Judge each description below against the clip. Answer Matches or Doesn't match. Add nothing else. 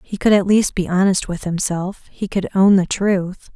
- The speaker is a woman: Matches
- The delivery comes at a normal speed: Doesn't match